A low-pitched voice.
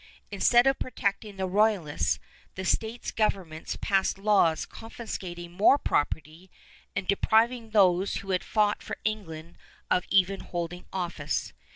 No: high, 195 Hz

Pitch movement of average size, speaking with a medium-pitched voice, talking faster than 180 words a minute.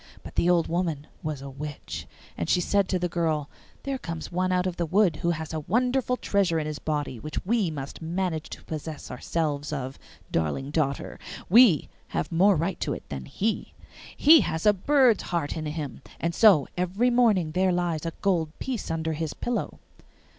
Yes: average, 4.0 semitones; medium, 165 Hz; average, 190 wpm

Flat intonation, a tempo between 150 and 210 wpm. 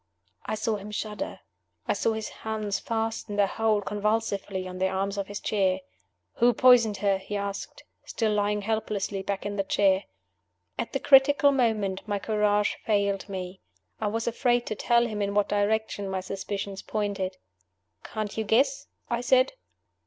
Yes: narrow, 1.9 semitones; average, 165 wpm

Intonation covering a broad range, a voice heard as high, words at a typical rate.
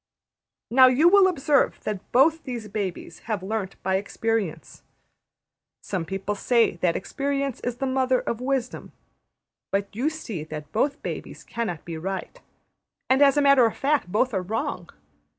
Yes: wide, 6.0 semitones; high, 230 Hz; average, 155 wpm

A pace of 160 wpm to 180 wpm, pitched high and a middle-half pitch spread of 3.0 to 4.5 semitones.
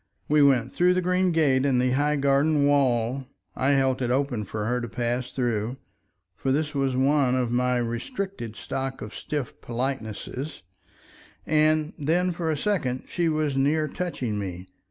No: average, 165 wpm; low, 135 Hz; average, 3.6 semitones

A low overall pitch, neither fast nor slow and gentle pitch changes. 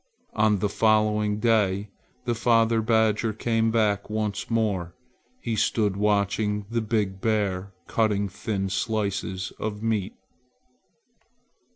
No: low, 105 Hz; slow, 110 wpm; narrow, 1.8 semitones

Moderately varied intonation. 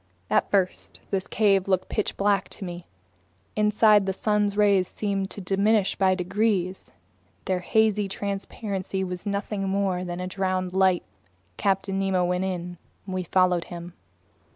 No: narrow, 1.7 semitones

